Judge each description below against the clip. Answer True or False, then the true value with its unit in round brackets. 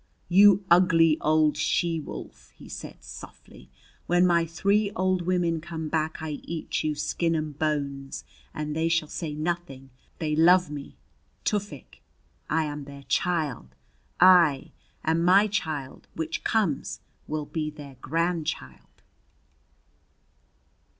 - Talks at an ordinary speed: False (125 wpm)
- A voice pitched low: False (160 Hz)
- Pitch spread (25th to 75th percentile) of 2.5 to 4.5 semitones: True (2.9 semitones)